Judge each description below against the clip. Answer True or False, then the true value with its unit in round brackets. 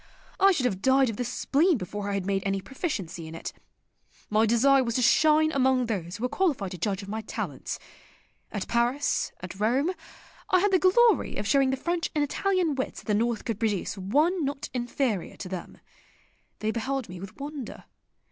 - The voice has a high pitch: True (245 Hz)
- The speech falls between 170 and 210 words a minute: True (195 wpm)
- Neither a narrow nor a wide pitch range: False (6.1 semitones)